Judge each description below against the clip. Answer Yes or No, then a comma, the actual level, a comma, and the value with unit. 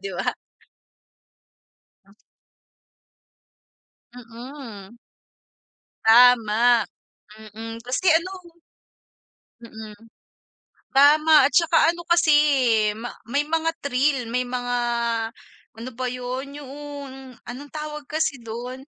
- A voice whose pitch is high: Yes, very high, 255 Hz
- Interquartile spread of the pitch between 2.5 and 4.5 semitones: Yes, average, 4.0 semitones